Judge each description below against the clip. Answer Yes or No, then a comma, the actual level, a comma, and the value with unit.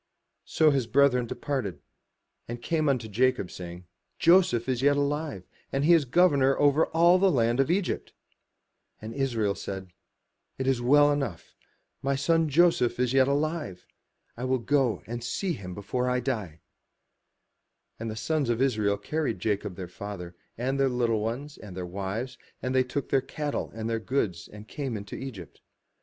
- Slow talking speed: No, average, 165 wpm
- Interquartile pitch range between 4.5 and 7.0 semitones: Yes, average, 4.8 semitones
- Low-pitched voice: Yes, low, 125 Hz